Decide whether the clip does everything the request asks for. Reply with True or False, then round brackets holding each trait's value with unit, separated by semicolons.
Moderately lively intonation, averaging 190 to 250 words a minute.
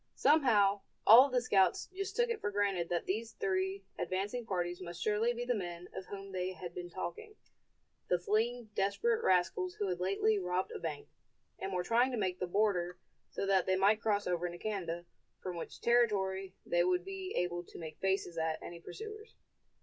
True (4.1 semitones; 195 wpm)